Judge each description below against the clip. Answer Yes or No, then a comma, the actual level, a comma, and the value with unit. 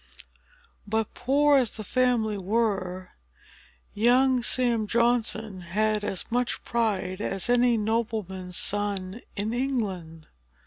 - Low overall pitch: No, high, 220 Hz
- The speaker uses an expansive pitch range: No, average, 3.8 semitones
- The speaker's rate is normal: No, slow, 105 wpm